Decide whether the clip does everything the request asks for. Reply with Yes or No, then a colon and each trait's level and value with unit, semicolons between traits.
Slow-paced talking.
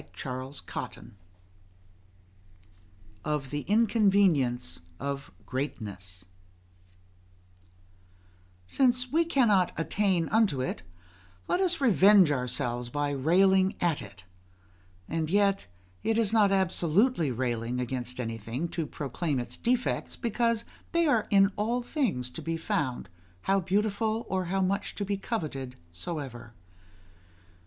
Yes: slow, 115 wpm